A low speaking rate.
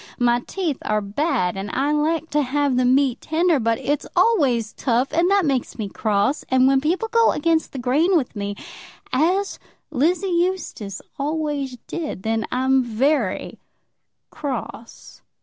No: average, 150 wpm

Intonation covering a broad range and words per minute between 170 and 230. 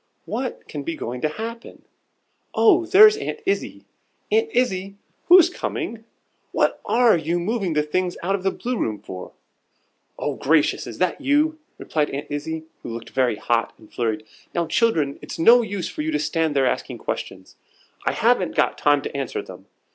Yes: wide, 8.7 semitones; average, 175 wpm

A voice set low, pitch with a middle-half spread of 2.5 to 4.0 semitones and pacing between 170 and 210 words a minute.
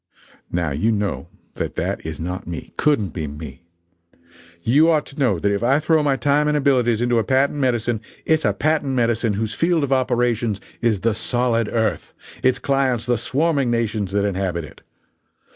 No: low, 120 Hz; average, 5.1 semitones; average, 180 wpm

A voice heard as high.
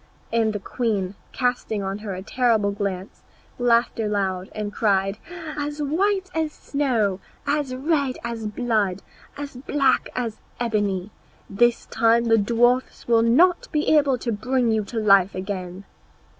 Yes: high, 230 Hz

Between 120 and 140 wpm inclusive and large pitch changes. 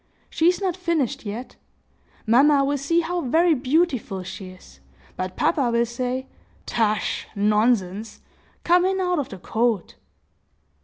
Yes: slow, 135 wpm; wide, 7.5 semitones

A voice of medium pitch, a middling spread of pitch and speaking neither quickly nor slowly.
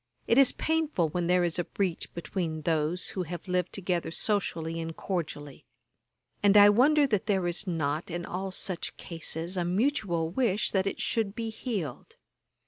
Yes: medium, 180 Hz; average, 3.7 semitones; average, 170 wpm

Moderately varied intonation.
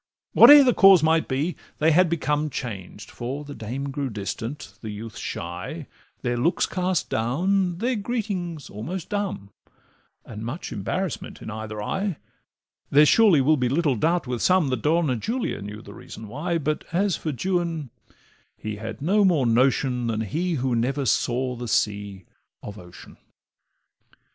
No: wide, 7.5 semitones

